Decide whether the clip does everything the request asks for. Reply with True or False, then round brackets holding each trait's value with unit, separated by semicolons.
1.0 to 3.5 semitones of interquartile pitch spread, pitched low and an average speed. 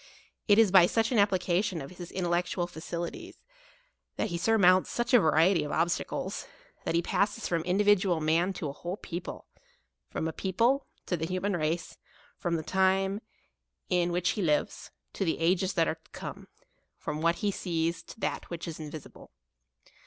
False (2.6 semitones; 175 Hz; 180 wpm)